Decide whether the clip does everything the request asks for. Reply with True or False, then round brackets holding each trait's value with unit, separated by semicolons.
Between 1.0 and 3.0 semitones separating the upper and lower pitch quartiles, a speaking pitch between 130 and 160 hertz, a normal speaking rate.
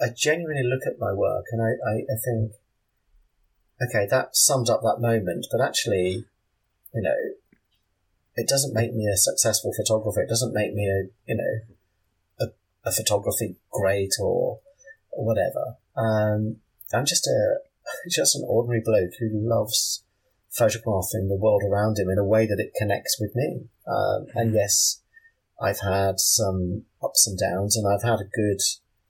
False (2.7 semitones; 105 Hz; 165 wpm)